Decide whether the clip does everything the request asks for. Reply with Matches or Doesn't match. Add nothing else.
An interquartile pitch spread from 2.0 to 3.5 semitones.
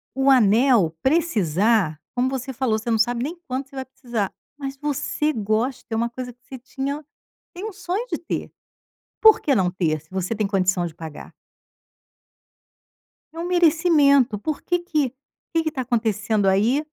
Doesn't match